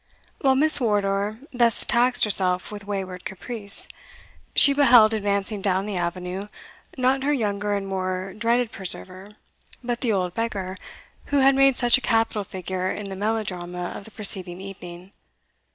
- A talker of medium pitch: No, high, 205 Hz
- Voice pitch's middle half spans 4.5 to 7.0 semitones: No, average, 3.9 semitones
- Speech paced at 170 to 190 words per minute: No, average, 150 wpm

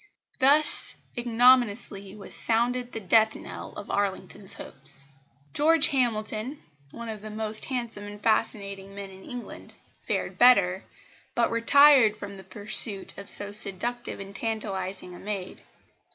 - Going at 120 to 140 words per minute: Yes, slow, 135 wpm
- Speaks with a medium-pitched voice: No, high, 215 Hz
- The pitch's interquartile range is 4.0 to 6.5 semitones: No, average, 3.3 semitones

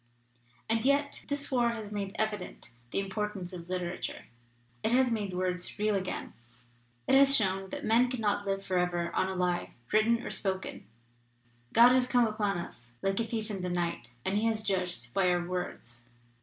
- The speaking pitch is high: Yes, high, 195 Hz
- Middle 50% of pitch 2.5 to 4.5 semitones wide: Yes, average, 3.9 semitones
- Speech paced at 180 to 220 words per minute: Yes, average, 190 wpm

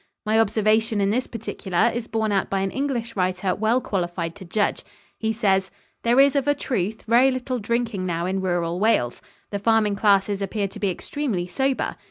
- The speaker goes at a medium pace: Yes, average, 190 wpm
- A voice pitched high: Yes, high, 215 Hz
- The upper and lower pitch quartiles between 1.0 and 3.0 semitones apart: No, average, 3.4 semitones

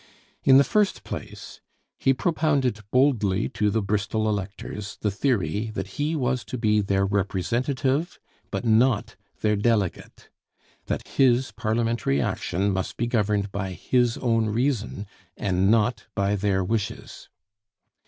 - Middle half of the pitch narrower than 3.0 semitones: No, average, 4.0 semitones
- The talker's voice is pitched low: Yes, low, 110 Hz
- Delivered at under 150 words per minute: Yes, slow, 135 wpm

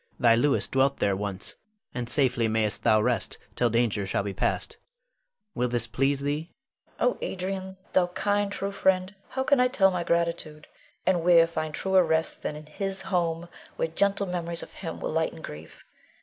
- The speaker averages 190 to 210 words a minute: No, average, 180 wpm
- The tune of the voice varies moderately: No, wide, 7.4 semitones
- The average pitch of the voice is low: No, medium, 160 Hz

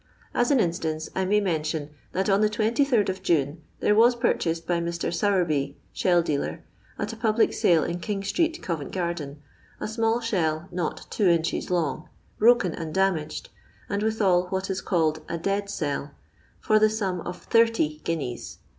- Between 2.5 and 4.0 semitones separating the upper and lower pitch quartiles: No, average, 4.7 semitones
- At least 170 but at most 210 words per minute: Yes, average, 180 wpm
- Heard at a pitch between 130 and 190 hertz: Yes, medium, 185 Hz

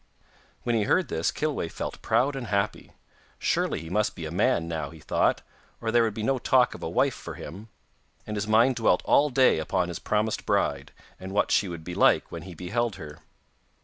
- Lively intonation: Yes, wide, 5.9 semitones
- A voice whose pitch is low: Yes, low, 105 Hz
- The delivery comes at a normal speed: No, fast, 215 wpm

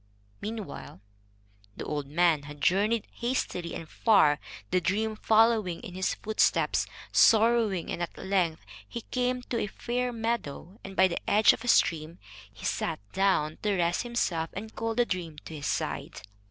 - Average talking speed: Yes, average, 165 wpm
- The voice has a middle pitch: No, high, 195 Hz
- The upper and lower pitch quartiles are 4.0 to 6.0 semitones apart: Yes, average, 5.1 semitones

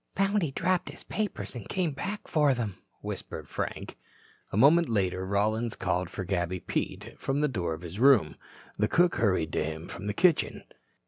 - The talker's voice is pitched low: Yes, low, 110 Hz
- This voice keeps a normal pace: Yes, average, 185 wpm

